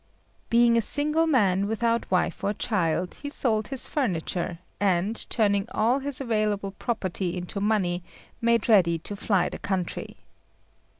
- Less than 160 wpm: Yes, average, 140 wpm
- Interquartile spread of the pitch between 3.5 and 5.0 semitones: Yes, average, 4.0 semitones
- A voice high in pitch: Yes, high, 210 Hz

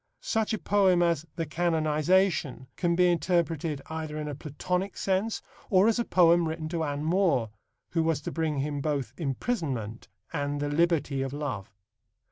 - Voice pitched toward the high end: No, medium, 160 Hz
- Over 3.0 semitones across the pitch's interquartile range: Yes, average, 3.4 semitones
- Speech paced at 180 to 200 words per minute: No, average, 165 wpm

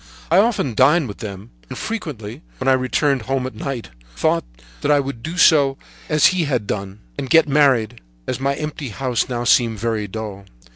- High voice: No, low, 130 Hz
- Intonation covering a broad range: No, average, 4.9 semitones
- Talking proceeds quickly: No, average, 185 wpm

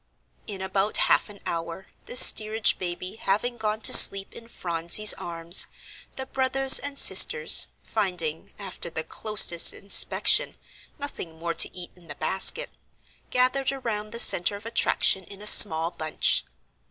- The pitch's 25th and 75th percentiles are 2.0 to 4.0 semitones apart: No, average, 5.0 semitones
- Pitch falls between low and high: No, high, 200 Hz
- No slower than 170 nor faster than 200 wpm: No, average, 145 wpm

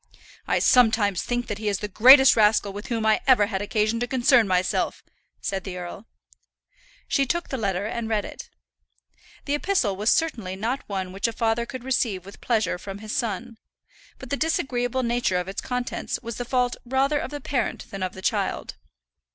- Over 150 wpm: Yes, average, 190 wpm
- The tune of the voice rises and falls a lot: No, average, 3.8 semitones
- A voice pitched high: Yes, high, 225 Hz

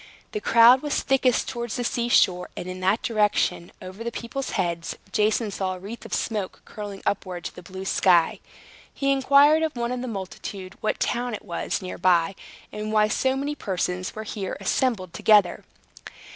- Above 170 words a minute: Yes, average, 185 wpm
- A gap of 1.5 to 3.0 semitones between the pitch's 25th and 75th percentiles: No, average, 4.7 semitones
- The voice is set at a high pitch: Yes, high, 210 Hz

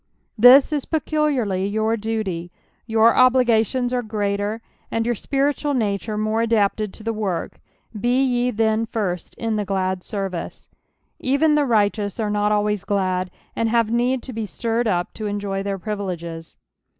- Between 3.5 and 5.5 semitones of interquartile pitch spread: No, average, 3.1 semitones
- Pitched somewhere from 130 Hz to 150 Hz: No, high, 220 Hz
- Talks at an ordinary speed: Yes, average, 160 wpm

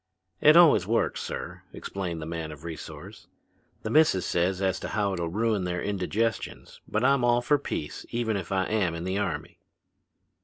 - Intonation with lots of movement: No, average, 4.7 semitones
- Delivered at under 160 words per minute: No, average, 175 wpm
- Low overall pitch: Yes, very low, 95 Hz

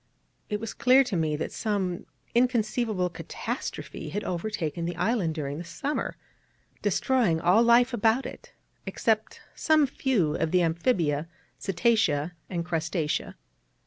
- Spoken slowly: Yes, slow, 130 wpm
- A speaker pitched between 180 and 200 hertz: Yes, high, 190 Hz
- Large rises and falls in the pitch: Yes, wide, 6.0 semitones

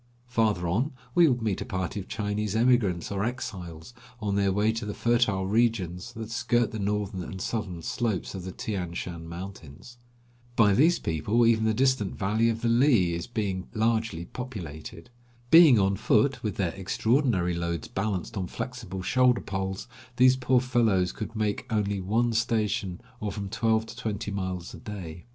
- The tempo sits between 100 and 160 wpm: No, average, 175 wpm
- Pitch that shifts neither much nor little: Yes, average, 3.8 semitones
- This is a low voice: Yes, low, 105 Hz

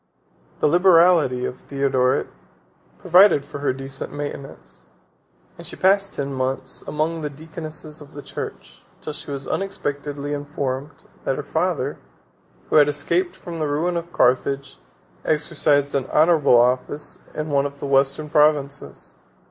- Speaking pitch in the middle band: Yes, medium, 145 Hz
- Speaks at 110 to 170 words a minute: Yes, average, 140 wpm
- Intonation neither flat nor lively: No, narrow, 2.3 semitones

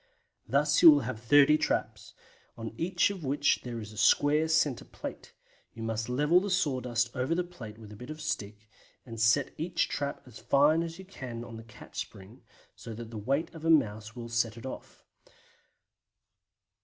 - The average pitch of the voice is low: Yes, low, 130 Hz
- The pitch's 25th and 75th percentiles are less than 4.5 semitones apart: No, average, 5.2 semitones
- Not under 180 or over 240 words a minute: Yes, average, 190 wpm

